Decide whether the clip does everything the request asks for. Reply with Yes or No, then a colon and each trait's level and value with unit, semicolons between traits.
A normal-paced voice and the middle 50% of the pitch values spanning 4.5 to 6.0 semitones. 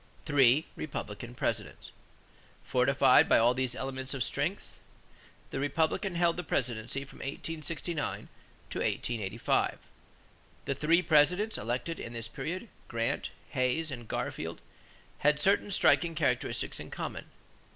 No: slow, 120 wpm; average, 4.9 semitones